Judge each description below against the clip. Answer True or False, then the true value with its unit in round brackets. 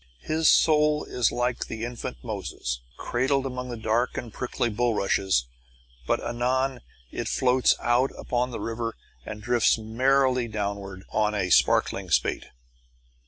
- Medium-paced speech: False (130 wpm)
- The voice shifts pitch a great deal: False (3.0 semitones)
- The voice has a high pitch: False (120 Hz)